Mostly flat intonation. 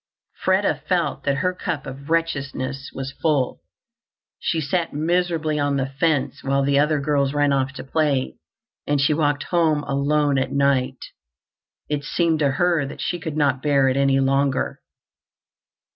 Yes: narrow, 2.1 semitones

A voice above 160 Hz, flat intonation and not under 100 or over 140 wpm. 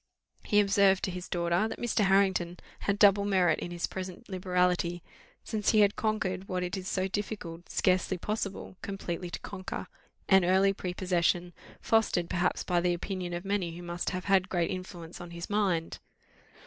No: medium, 185 Hz; narrow, 2.1 semitones; average, 175 wpm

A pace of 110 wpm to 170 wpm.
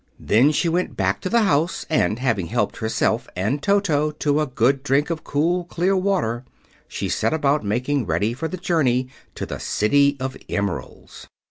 No: average, 185 wpm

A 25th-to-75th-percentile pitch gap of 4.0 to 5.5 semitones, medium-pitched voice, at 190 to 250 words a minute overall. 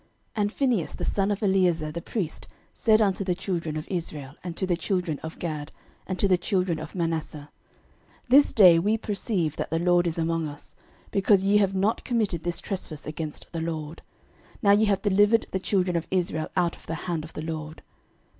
No: average, 3.6 semitones; medium, 175 Hz; average, 200 wpm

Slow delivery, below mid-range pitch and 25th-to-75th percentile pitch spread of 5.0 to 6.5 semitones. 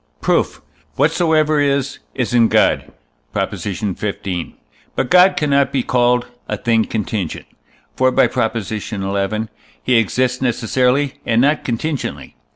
No: slow, 125 wpm; low, 125 Hz; average, 4.1 semitones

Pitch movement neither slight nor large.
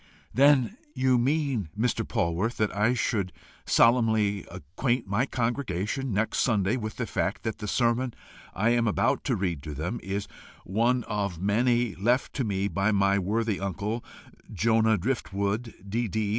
Yes: average, 3.5 semitones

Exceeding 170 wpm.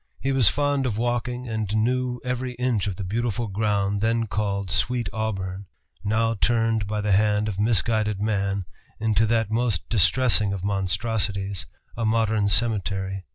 No: average, 155 wpm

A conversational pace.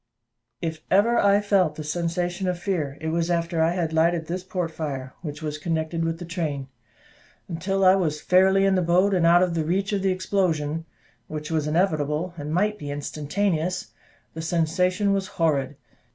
Yes: average, 180 wpm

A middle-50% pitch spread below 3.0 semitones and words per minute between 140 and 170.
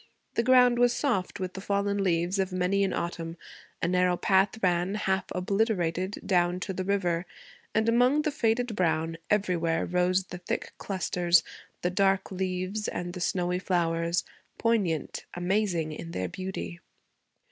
Yes: narrow, 2.4 semitones; average, 150 wpm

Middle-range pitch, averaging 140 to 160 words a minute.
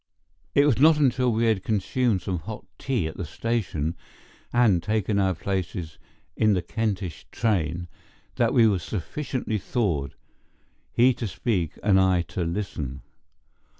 No: low, 100 Hz; average, 145 wpm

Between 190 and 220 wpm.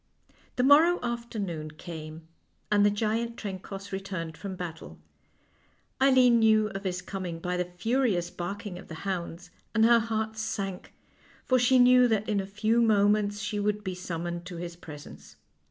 No: average, 160 wpm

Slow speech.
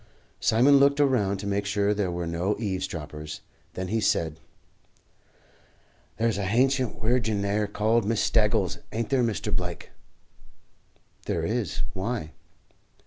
Yes: slow, 130 wpm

